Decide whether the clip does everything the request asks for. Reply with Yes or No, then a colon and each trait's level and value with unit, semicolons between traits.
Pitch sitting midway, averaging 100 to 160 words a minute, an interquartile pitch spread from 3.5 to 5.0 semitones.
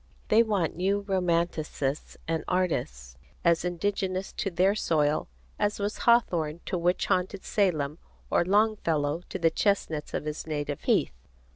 Yes: medium, 175 Hz; average, 140 wpm; average, 4.2 semitones